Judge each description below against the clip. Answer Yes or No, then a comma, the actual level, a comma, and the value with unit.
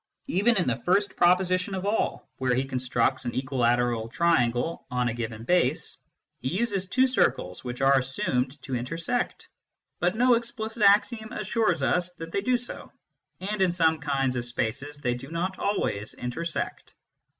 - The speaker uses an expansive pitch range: Yes, wide, 7.5 semitones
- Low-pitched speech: No, medium, 160 Hz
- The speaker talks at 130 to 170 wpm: Yes, average, 160 wpm